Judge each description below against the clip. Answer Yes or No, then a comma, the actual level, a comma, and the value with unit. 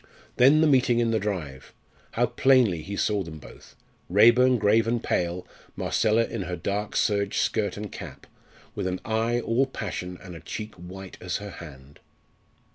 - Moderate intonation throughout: Yes, average, 4.4 semitones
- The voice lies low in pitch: Yes, low, 105 Hz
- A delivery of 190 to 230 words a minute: No, average, 170 wpm